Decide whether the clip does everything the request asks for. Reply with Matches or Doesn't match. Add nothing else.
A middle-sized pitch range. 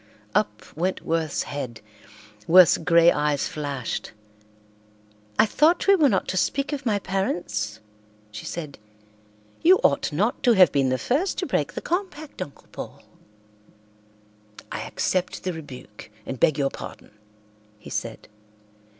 Doesn't match